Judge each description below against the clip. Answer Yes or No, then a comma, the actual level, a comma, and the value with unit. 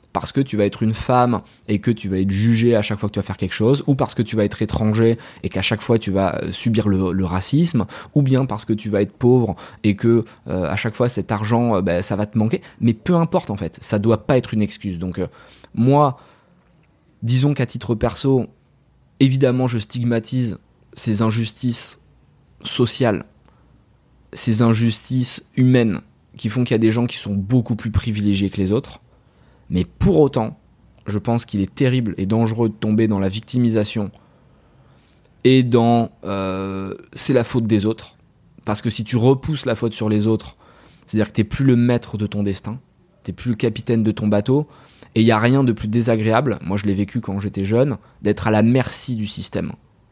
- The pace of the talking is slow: No, average, 205 wpm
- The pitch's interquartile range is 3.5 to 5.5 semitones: No, average, 3.0 semitones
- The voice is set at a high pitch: No, low, 110 Hz